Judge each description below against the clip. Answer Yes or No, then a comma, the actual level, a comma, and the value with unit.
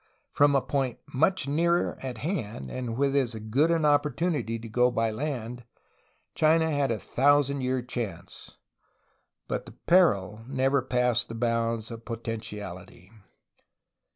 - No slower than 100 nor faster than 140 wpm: Yes, slow, 135 wpm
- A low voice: Yes, low, 125 Hz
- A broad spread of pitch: No, average, 4.1 semitones